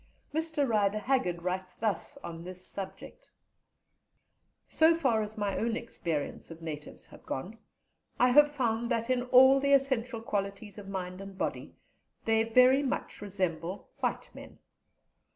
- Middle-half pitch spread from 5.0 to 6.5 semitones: Yes, wide, 5.4 semitones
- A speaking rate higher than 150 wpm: No, average, 145 wpm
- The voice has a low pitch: No, high, 220 Hz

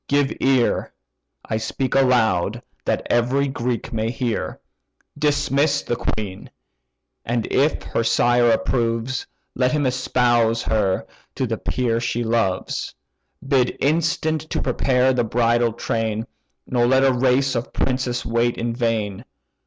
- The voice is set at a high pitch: No, low, 120 Hz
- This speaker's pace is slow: Yes, slow, 130 wpm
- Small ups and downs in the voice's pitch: Yes, narrow, 2.3 semitones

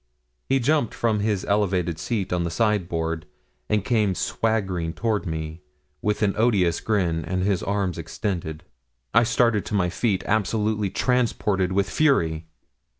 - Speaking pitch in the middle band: No, low, 100 Hz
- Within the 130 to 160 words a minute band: Yes, average, 145 wpm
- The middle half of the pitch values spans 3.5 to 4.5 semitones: Yes, average, 3.8 semitones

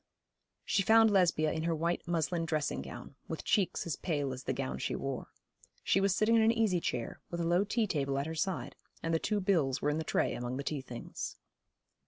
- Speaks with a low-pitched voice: No, medium, 165 Hz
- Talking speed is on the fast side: Yes, fast, 225 wpm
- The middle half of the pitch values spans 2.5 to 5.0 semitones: No, wide, 5.5 semitones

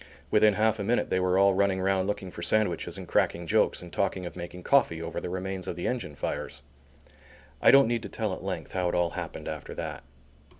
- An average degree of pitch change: Yes, average, 3.0 semitones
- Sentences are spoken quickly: Yes, fast, 225 wpm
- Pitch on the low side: Yes, very low, 95 Hz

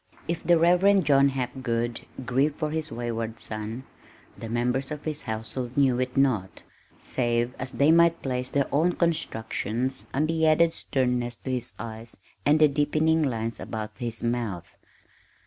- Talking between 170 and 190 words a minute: No, average, 155 wpm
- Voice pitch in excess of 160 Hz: No, low, 130 Hz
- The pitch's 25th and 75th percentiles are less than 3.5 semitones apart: No, average, 4.4 semitones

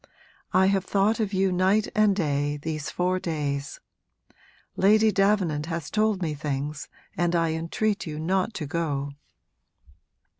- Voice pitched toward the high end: No, medium, 175 Hz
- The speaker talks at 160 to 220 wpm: No, average, 140 wpm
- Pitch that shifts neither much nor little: Yes, average, 4.5 semitones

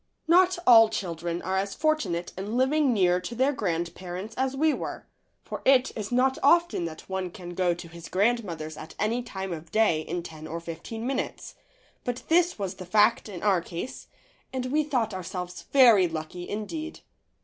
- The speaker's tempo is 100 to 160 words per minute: No, average, 180 wpm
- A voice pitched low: No, high, 200 Hz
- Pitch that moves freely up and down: Yes, wide, 6.5 semitones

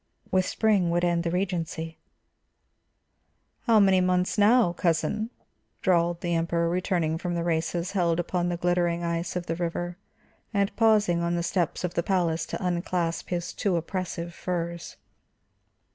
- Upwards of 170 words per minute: No, average, 150 wpm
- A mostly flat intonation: Yes, narrow, 1.4 semitones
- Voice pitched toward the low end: No, medium, 175 Hz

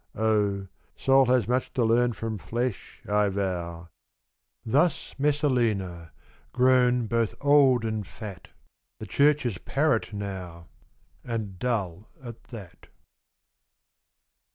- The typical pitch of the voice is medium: No, low, 110 Hz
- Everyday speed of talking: No, slow, 105 wpm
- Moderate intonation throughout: Yes, average, 4.3 semitones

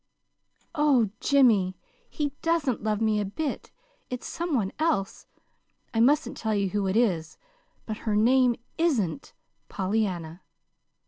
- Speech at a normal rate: No, slow, 130 wpm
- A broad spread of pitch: Yes, wide, 5.7 semitones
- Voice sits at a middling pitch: No, high, 220 Hz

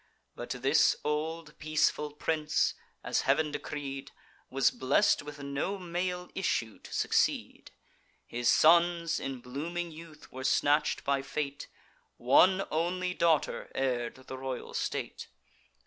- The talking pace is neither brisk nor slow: No, slow, 120 wpm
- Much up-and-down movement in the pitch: No, average, 3.8 semitones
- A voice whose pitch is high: No, medium, 150 Hz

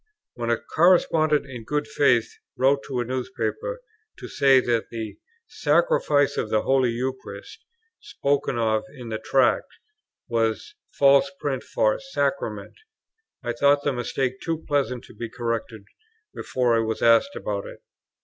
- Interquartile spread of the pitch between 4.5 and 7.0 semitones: No, average, 3.8 semitones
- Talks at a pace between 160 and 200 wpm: No, average, 150 wpm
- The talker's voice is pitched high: No, low, 130 Hz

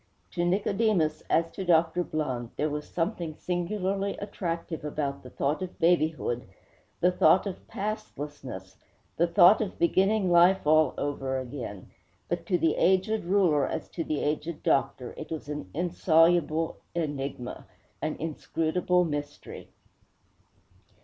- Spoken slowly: Yes, slow, 130 wpm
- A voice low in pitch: No, medium, 165 Hz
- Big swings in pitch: No, average, 3.5 semitones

